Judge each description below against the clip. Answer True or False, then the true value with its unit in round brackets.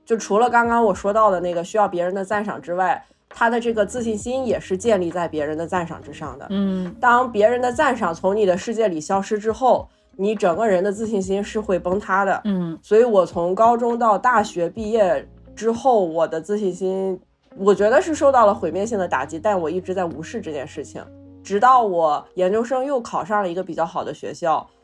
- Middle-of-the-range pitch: False (200 Hz)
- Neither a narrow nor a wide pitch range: True (3.9 semitones)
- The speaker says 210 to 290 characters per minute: False (315 characters per minute)